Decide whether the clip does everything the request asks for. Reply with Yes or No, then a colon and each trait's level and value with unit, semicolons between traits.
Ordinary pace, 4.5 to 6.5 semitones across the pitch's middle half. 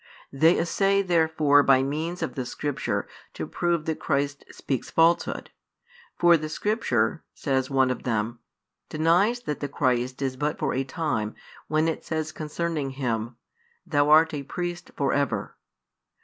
No: average, 150 wpm; average, 3.7 semitones